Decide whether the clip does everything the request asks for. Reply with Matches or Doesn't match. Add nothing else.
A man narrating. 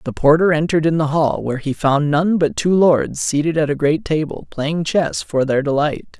Matches